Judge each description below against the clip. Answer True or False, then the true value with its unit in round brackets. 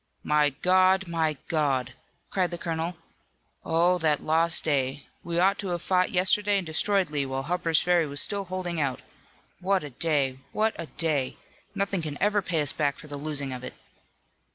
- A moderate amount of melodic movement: True (3.8 semitones)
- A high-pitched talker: False (165 Hz)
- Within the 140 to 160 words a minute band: False (180 wpm)